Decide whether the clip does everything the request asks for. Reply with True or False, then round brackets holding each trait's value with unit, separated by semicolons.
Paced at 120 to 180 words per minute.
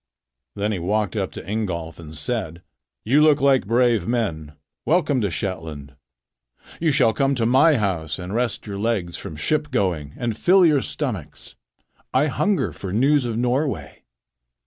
True (160 wpm)